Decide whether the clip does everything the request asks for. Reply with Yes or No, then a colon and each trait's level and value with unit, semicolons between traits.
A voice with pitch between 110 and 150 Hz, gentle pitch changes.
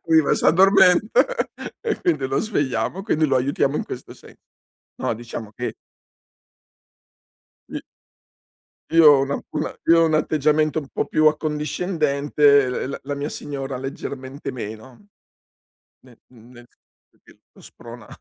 No: medium, 140 Hz; average, 3.2 semitones